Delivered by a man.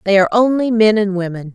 No: female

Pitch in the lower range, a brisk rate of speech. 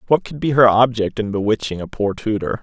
Yes: low, 115 Hz; fast, 230 wpm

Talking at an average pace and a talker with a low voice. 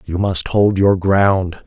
Yes: average, 180 wpm; very low, 95 Hz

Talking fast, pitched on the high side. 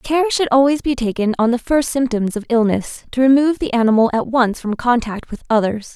Yes: fast, 210 wpm; high, 245 Hz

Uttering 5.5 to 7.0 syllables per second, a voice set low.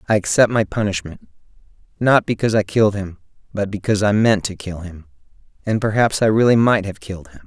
Yes: 6.2 syllables/s; low, 100 Hz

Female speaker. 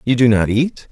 No: male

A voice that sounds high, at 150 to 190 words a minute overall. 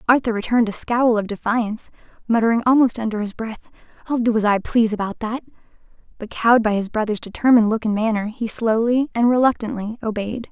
Yes: high, 225 Hz; average, 185 wpm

